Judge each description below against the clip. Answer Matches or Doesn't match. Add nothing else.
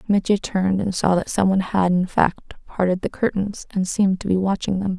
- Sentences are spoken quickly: Matches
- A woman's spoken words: Matches